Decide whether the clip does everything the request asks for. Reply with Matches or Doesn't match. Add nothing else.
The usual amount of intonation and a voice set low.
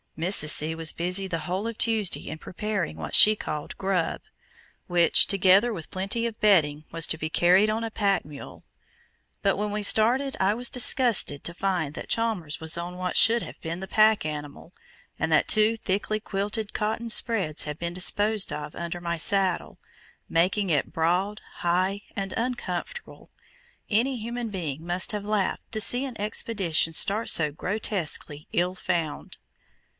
Doesn't match